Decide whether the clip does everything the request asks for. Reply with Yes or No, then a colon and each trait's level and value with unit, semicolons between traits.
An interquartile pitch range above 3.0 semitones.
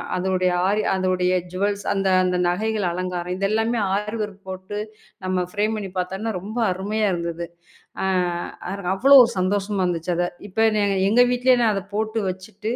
No: narrow, 2.6 semitones